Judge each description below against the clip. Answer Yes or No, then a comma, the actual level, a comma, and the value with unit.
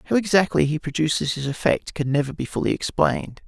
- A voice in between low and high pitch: Yes, medium, 150 Hz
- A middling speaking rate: Yes, average, 190 wpm